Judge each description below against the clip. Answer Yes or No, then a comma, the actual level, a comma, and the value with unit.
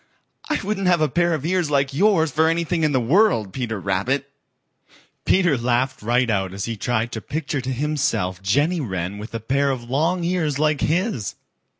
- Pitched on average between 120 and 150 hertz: Yes, medium, 140 Hz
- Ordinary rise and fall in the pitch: No, wide, 6.0 semitones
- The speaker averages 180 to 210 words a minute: Yes, average, 190 wpm